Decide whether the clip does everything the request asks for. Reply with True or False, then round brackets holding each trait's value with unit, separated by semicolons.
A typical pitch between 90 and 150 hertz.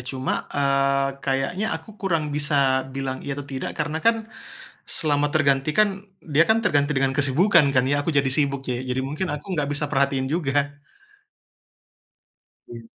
True (140 Hz)